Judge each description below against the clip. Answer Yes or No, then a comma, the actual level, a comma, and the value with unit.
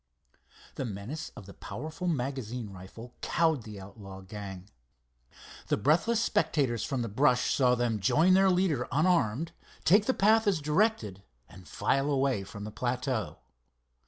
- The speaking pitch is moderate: No, low, 125 Hz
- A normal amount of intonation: No, wide, 7.4 semitones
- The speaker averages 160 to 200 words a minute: No, average, 145 wpm